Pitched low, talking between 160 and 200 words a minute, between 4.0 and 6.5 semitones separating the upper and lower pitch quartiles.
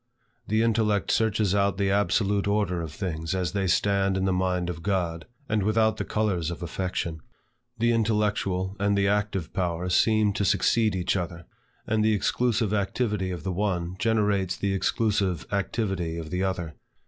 No: low, 100 Hz; average, 170 wpm; average, 2.7 semitones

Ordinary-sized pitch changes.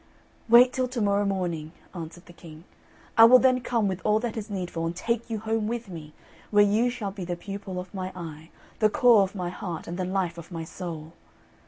Yes: average, 4.4 semitones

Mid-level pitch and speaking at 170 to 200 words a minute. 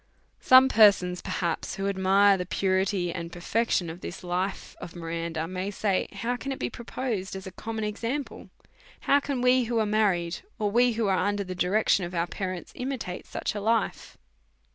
No: high, 200 Hz; average, 185 wpm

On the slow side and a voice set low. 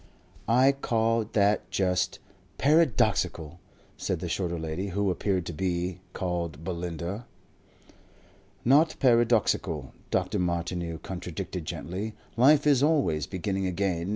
Yes: slow, 110 wpm; very low, 95 Hz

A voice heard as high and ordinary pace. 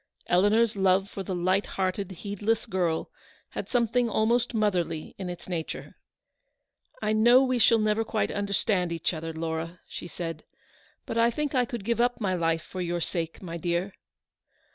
Yes: high, 195 Hz; average, 175 wpm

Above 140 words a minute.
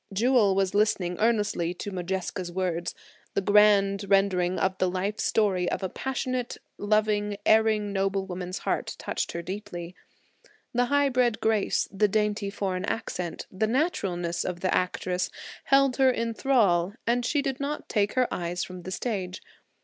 Yes: average, 155 wpm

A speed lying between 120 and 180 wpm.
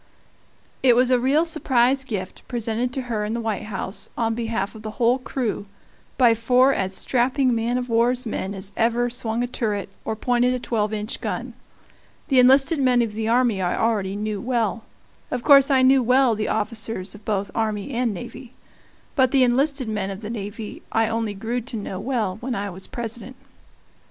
No: average, 190 wpm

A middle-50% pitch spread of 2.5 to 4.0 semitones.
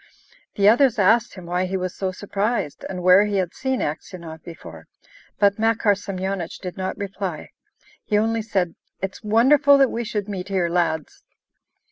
Yes: average, 3.2 semitones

